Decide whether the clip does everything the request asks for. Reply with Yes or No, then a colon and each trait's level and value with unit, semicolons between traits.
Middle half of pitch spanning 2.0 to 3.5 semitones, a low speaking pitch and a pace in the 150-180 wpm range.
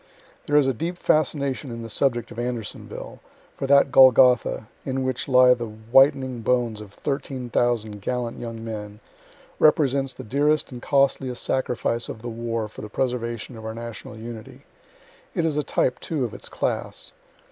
Yes: average, 2.8 semitones; low, 125 Hz; average, 165 wpm